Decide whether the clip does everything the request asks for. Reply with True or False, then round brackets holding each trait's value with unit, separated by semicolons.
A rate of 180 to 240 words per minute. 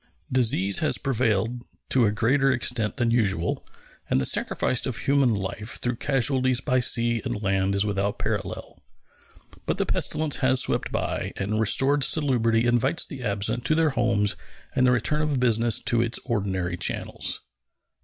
False (160 wpm)